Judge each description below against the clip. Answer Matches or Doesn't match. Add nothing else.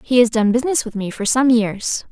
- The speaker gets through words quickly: Matches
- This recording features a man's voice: Doesn't match